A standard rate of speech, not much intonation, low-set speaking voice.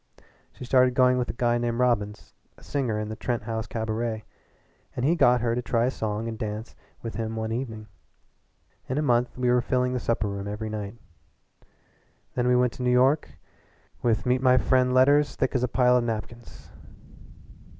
Yes: average, 190 wpm; narrow, 2.2 semitones; low, 120 Hz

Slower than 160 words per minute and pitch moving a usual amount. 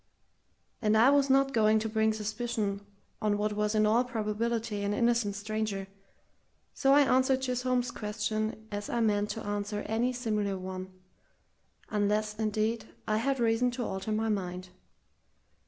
No: average, 150 wpm; narrow, 2.3 semitones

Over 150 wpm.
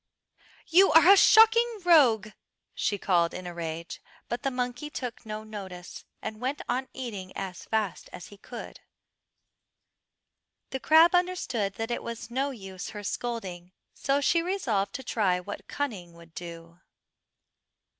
No: average, 145 wpm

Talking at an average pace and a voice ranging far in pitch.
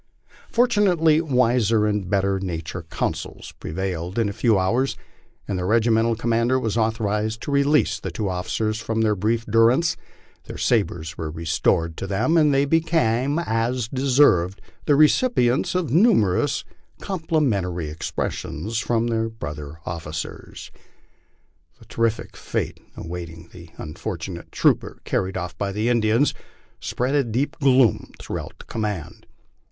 Yes: average, 145 wpm; wide, 5.8 semitones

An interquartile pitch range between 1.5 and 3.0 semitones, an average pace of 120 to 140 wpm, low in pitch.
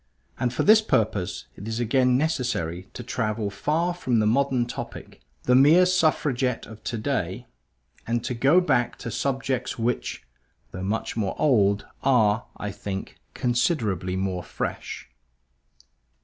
No: average, 4.5 semitones; slow, 135 wpm; low, 120 Hz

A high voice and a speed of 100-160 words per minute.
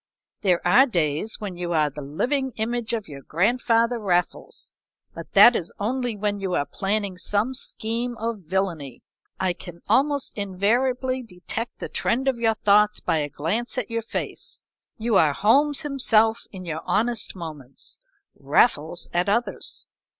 Yes: high, 210 Hz; average, 155 wpm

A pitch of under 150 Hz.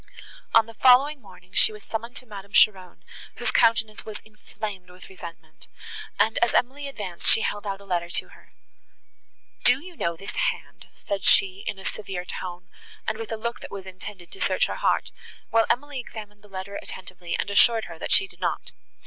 No: high, 205 Hz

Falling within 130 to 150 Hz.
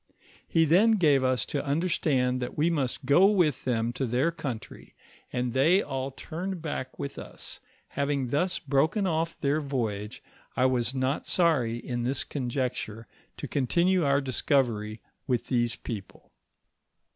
Yes: low, 135 Hz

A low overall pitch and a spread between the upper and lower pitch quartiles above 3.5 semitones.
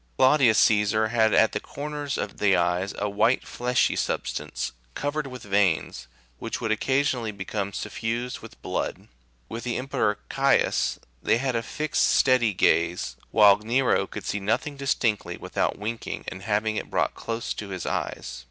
Yes: low, 110 Hz; average, 4.0 semitones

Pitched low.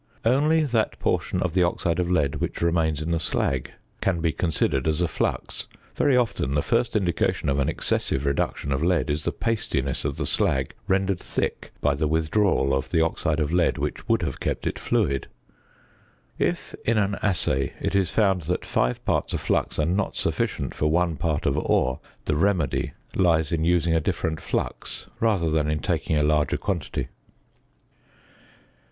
Yes: very low, 80 Hz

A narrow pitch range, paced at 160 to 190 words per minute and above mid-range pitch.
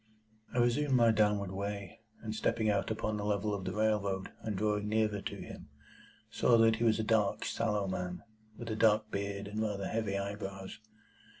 No: narrow, 1.7 semitones; average, 185 wpm; low, 105 Hz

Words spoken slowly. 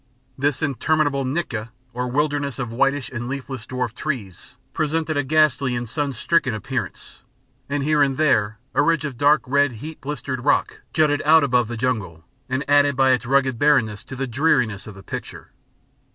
No: average, 175 wpm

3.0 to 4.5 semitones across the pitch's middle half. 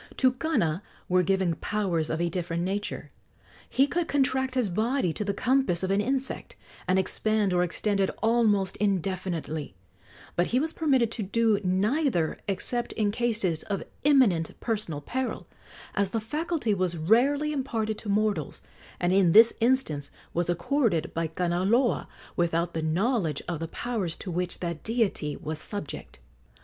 No: wide, 5.6 semitones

